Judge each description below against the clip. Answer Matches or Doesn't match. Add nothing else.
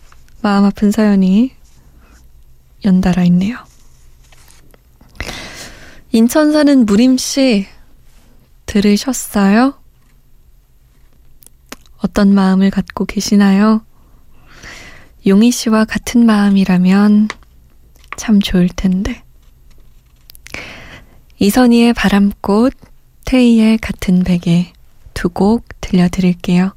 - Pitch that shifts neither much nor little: Matches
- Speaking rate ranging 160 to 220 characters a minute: Matches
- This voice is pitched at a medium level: Doesn't match